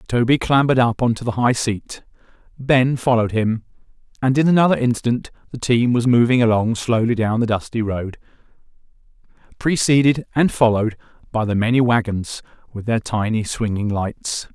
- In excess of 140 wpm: Yes, average, 155 wpm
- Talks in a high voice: No, low, 120 Hz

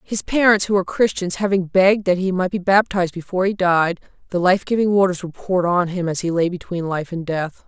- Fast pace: Yes, fast, 235 wpm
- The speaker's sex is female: Yes, female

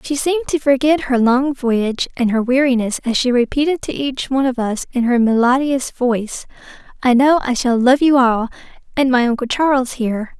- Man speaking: No, female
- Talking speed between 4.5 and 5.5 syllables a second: Yes, 5.3 syllables/s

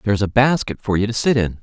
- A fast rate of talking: Yes, fast, 295 wpm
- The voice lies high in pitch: No, low, 110 Hz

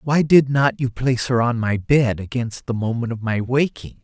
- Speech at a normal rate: No, fast, 225 wpm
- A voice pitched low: Yes, low, 120 Hz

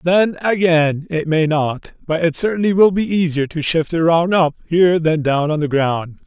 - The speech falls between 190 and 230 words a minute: Yes, average, 200 wpm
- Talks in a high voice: No, medium, 165 Hz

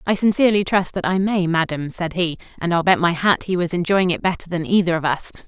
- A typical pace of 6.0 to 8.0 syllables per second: Yes, 6.1 syllables/s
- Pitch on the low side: No, medium, 175 Hz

